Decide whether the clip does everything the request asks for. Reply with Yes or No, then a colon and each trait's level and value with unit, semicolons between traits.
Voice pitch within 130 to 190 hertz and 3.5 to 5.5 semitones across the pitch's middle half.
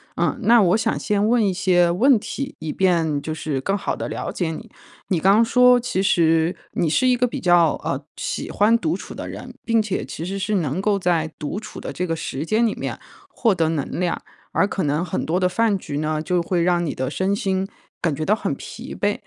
Yes: medium, 185 Hz; average, 4.7 semitones